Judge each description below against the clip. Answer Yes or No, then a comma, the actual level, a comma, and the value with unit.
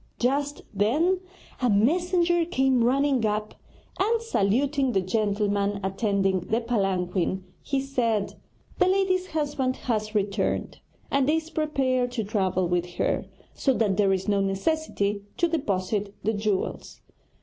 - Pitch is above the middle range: Yes, high, 225 Hz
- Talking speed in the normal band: No, slow, 130 wpm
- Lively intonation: Yes, wide, 6.2 semitones